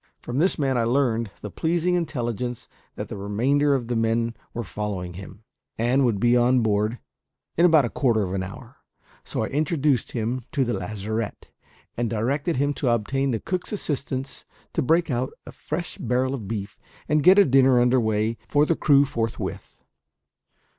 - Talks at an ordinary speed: Yes, average, 180 wpm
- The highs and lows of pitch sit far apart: No, average, 4.2 semitones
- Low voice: Yes, low, 125 Hz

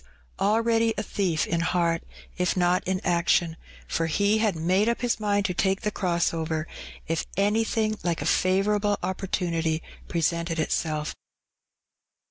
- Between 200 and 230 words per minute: No, average, 140 wpm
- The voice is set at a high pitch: No, medium, 180 Hz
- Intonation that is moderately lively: Yes, average, 3.7 semitones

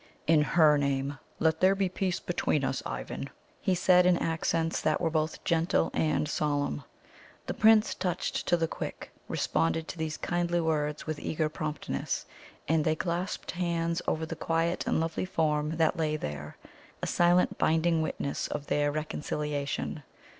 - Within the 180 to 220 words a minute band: No, average, 160 wpm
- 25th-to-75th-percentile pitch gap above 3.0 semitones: No, narrow, 2.4 semitones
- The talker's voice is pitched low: No, medium, 160 Hz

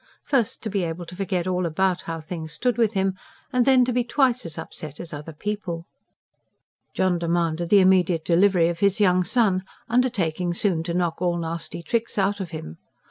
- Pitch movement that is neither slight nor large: Yes, average, 3.4 semitones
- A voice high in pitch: No, medium, 180 Hz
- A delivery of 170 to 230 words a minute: Yes, average, 190 wpm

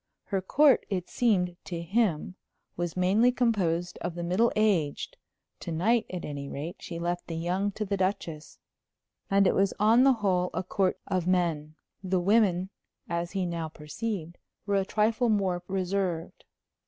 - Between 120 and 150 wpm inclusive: No, average, 165 wpm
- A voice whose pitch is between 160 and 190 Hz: Yes, medium, 185 Hz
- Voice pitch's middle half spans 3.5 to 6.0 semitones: No, average, 3.0 semitones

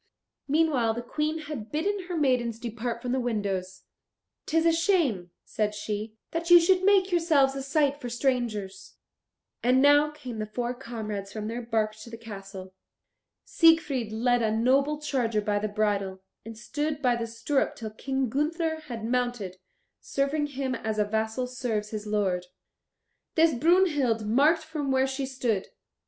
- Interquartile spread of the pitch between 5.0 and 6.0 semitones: Yes, wide, 5.4 semitones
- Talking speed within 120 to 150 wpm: No, average, 160 wpm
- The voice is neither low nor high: No, high, 245 Hz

